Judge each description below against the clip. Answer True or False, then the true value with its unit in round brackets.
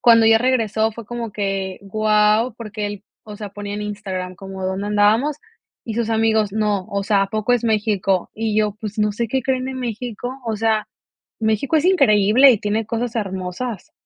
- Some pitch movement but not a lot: False (2.1 semitones)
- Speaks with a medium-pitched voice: False (215 Hz)